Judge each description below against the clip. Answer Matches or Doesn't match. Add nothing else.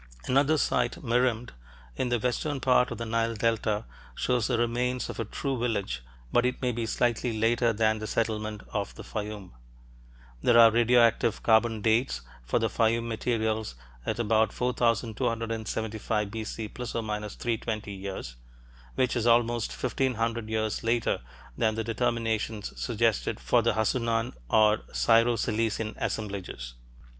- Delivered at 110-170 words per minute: Matches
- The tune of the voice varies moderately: Doesn't match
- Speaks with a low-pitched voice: Matches